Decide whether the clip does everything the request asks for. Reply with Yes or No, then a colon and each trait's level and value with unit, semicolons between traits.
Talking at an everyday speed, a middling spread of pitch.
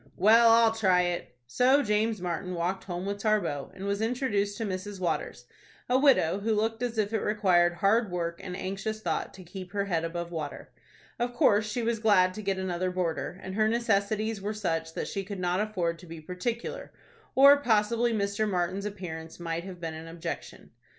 Yes: average, 190 wpm; average, 3.6 semitones